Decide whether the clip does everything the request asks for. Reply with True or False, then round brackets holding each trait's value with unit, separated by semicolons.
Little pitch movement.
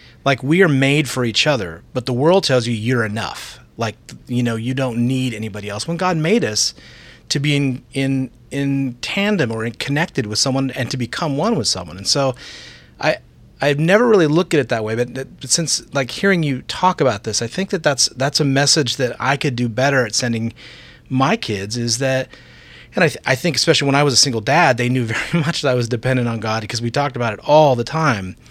False (3.4 semitones)